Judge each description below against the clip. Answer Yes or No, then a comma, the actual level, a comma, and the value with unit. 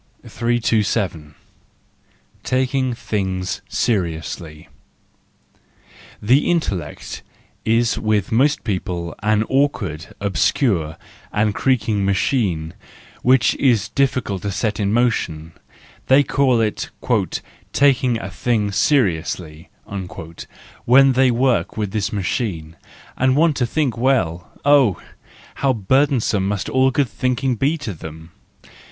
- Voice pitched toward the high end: No, low, 110 Hz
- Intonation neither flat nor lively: No, wide, 5.7 semitones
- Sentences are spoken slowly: Yes, slow, 105 wpm